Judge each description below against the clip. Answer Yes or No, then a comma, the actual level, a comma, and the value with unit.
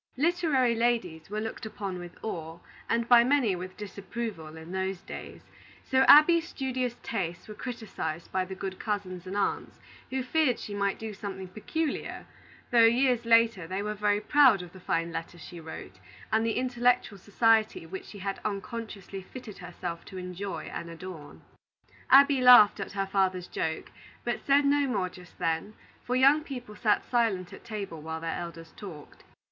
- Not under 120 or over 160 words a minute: No, average, 170 wpm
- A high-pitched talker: Yes, high, 205 Hz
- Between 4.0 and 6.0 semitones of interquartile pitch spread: Yes, average, 4.8 semitones